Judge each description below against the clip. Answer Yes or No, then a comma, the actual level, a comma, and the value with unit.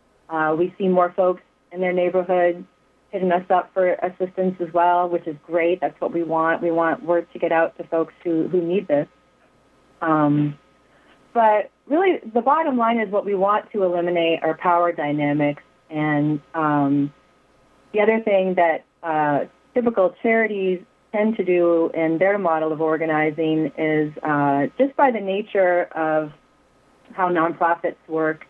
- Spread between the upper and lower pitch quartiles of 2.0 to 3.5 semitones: Yes, average, 3.2 semitones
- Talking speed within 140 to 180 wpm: Yes, average, 160 wpm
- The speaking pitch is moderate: Yes, medium, 175 Hz